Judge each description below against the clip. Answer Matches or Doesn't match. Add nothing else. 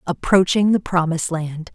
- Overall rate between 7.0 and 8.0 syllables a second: Doesn't match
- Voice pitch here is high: Doesn't match